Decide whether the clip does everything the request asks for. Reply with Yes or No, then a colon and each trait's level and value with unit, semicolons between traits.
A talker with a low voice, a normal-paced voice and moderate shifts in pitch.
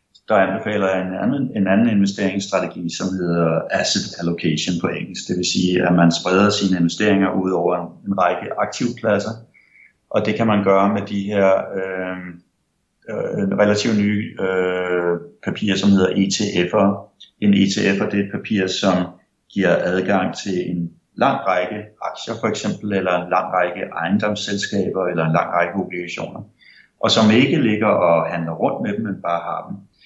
No: very low, 95 Hz; average, 165 wpm; narrow, 2.3 semitones